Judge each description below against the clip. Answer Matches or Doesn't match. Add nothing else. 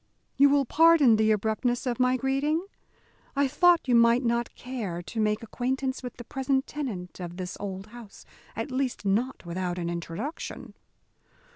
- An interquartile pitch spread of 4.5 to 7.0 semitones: Matches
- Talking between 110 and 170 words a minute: Matches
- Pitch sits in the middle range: Doesn't match